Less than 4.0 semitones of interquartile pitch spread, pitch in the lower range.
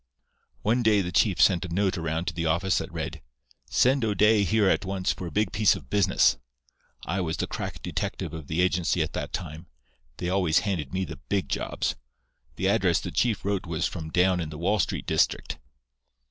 Yes: average, 3.6 semitones; very low, 90 Hz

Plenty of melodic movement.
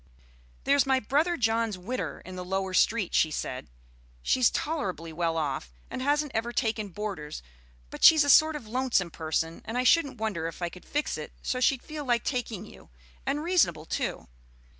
Yes: wide, 7.7 semitones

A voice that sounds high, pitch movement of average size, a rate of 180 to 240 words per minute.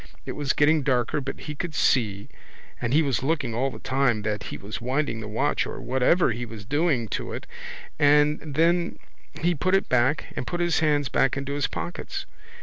No: medium, 140 Hz; average, 4.2 semitones; average, 200 wpm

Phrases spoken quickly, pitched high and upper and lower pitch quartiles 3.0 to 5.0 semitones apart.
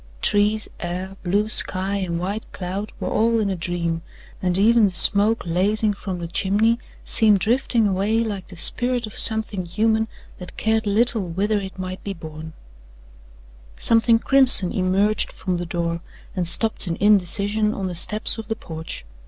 No: average, 165 wpm; high, 200 Hz; average, 3.3 semitones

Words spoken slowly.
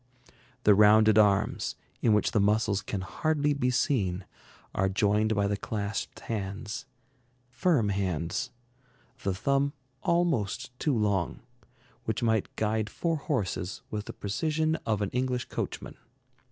Yes: slow, 130 wpm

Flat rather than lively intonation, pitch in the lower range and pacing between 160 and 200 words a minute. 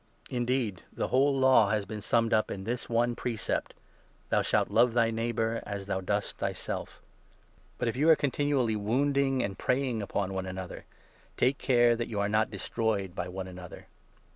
No: average, 3.7 semitones; low, 115 Hz; average, 190 wpm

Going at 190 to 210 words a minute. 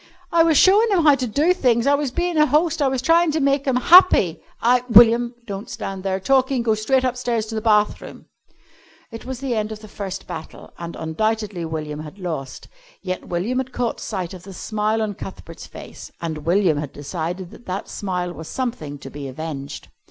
Yes: fast, 205 wpm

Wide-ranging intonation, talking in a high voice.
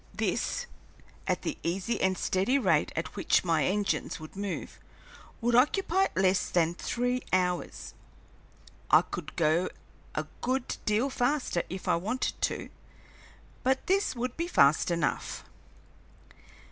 Yes: wide, 6.5 semitones; high, 195 Hz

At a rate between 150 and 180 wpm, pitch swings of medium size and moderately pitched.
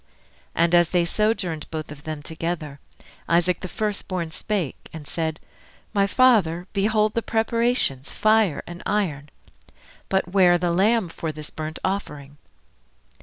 No: average, 140 wpm; average, 4.8 semitones; medium, 175 Hz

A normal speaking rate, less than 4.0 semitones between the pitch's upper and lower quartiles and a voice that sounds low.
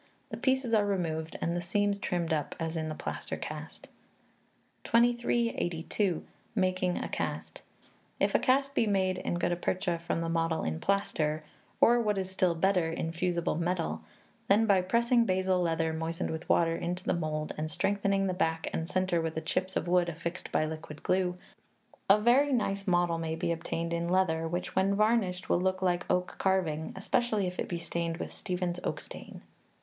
No: average, 180 wpm; average, 3.0 semitones; medium, 180 Hz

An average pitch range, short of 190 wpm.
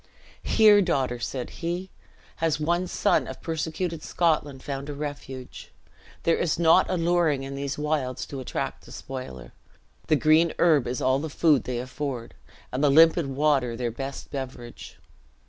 Yes: average, 3.8 semitones; average, 155 wpm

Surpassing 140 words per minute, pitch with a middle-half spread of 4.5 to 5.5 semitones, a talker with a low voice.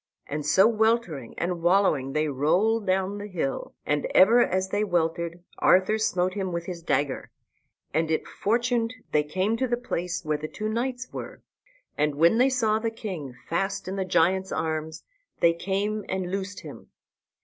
No: average, 170 wpm; average, 4.9 semitones; medium, 185 Hz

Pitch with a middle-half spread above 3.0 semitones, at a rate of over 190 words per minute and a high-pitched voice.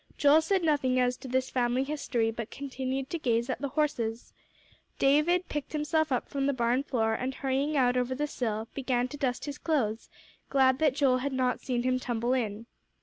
No: narrow, 2.6 semitones; average, 200 wpm; very high, 260 Hz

